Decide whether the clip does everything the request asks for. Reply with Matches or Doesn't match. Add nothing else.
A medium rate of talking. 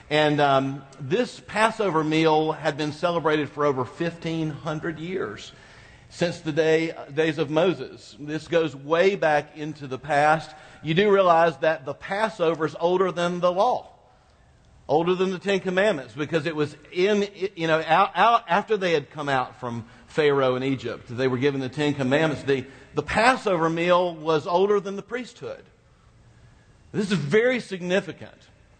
Matches